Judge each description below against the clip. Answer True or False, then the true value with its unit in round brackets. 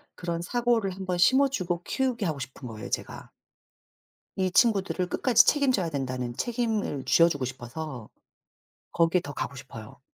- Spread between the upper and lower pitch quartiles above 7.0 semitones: True (8.7 semitones)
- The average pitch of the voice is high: False (175 Hz)